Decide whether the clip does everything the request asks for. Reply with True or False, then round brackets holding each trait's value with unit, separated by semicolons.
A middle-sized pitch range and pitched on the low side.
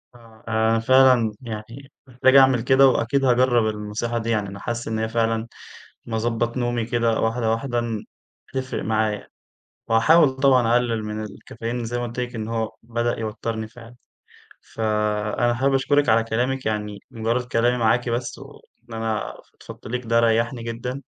False (1.8 semitones; 115 Hz)